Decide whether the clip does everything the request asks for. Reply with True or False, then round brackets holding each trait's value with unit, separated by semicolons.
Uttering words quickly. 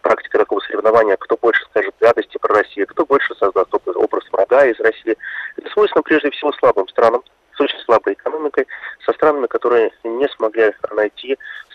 True (165 wpm)